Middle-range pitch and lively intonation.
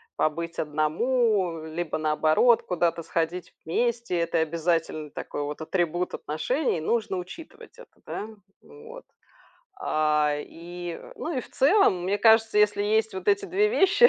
Yes: medium, 180 Hz; wide, 6.5 semitones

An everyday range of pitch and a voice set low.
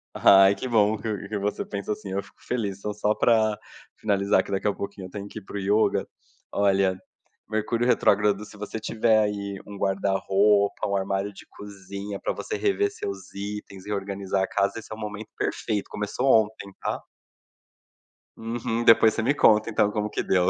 No: narrow, 1.6 semitones; low, 105 Hz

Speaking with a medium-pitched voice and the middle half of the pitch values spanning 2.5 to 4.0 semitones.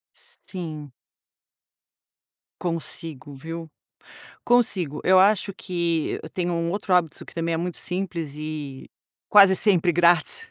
Yes: medium, 175 Hz; average, 2.8 semitones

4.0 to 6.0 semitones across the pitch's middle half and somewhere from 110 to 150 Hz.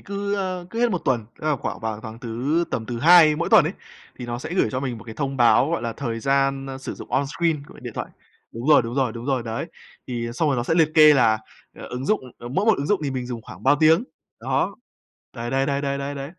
Yes: average, 4.7 semitones; low, 135 Hz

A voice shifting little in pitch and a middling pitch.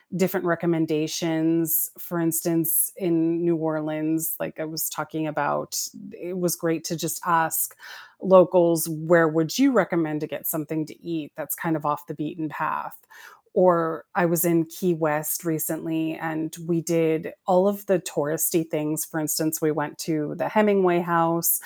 Yes: narrow, 1.5 semitones; medium, 165 Hz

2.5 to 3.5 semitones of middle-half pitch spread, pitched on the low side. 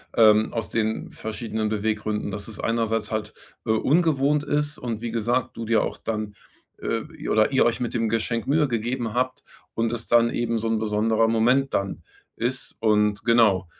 No: narrow, 1.8 semitones; low, 115 Hz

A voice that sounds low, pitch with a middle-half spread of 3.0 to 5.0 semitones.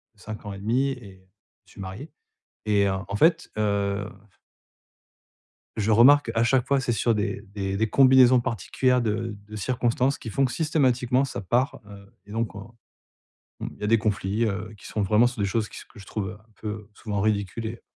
Yes: low, 110 Hz; average, 3.4 semitones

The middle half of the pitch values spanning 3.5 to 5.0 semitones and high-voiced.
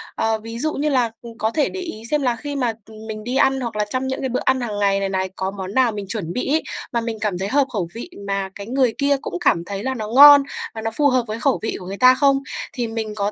Yes: average, 4.1 semitones; high, 230 Hz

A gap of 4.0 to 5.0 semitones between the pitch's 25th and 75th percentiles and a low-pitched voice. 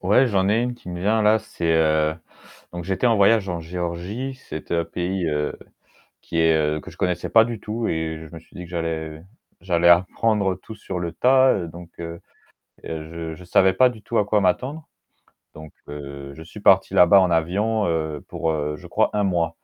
Yes: average, 4.3 semitones; very low, 90 Hz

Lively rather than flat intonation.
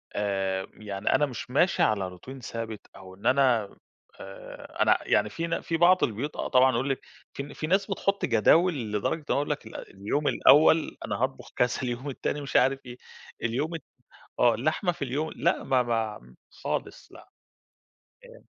Yes: wide, 5.8 semitones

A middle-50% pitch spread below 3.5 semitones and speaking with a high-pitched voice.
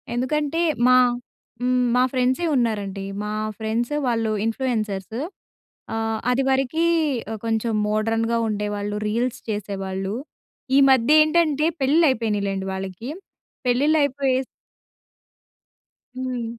No: average, 3.8 semitones; high, 235 Hz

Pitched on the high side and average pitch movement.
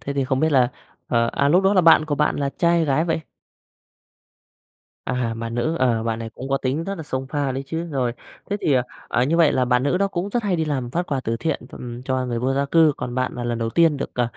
No: low, 135 Hz; average, 4.6 semitones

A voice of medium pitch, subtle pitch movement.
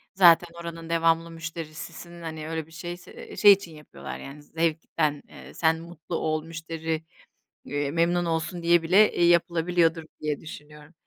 Yes: medium, 165 Hz; narrow, 1.3 semitones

